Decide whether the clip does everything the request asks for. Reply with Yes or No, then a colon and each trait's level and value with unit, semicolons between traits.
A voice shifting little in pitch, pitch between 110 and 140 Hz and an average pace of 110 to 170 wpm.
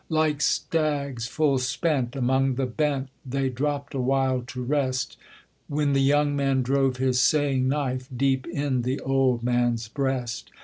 Yes: narrow, 1.9 semitones; low, 135 Hz; average, 150 wpm